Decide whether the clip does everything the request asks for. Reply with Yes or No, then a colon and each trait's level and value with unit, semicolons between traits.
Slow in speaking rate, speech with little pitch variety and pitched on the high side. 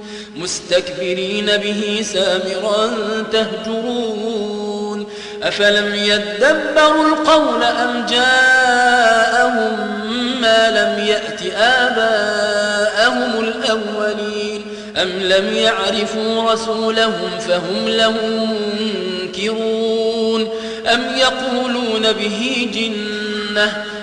Yes: slow, 60 wpm; narrow, 1.4 semitones; high, 220 Hz